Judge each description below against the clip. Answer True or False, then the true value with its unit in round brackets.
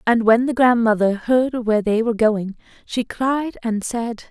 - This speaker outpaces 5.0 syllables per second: False (4.5 syllables/s)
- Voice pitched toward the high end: True (230 Hz)